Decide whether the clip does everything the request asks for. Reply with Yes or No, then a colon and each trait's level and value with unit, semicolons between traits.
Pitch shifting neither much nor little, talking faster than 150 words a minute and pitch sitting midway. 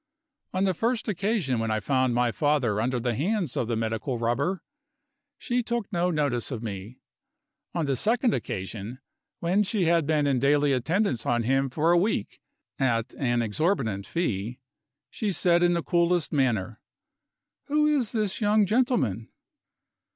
No: wide, 8.1 semitones; average, 160 wpm; medium, 145 Hz